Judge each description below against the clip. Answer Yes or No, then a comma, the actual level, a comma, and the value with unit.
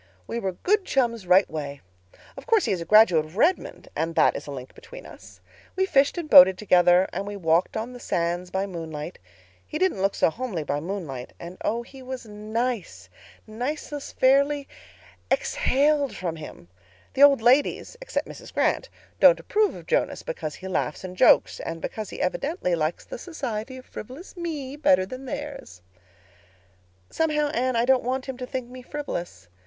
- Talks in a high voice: Yes, high, 235 Hz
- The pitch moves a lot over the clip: Yes, wide, 7.9 semitones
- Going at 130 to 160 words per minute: No, average, 175 wpm